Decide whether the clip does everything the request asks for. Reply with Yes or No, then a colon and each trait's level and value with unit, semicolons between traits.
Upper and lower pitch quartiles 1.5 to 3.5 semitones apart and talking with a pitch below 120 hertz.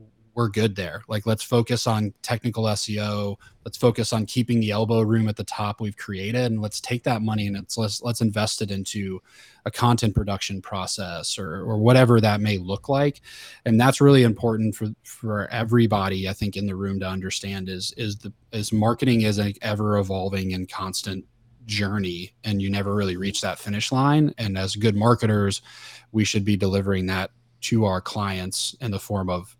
Yes: average, 2.8 semitones; low, 105 Hz